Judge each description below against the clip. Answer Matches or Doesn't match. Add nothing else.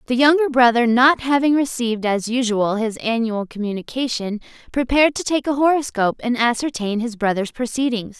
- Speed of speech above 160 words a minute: Doesn't match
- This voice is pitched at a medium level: Doesn't match